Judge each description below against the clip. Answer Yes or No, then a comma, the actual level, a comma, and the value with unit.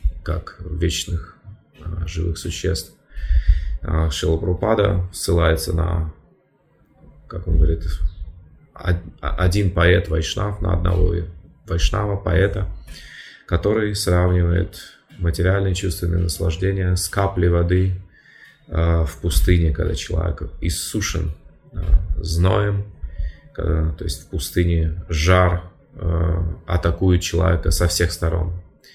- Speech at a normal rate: No, slow, 85 wpm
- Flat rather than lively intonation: Yes, narrow, 2.0 semitones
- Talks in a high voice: No, very low, 85 Hz